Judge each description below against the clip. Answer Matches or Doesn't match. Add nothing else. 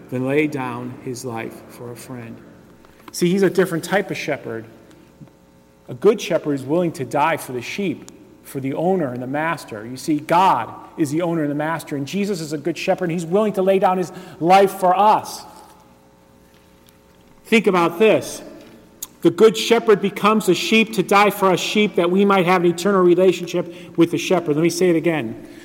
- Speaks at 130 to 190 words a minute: Doesn't match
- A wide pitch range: Matches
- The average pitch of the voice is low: Doesn't match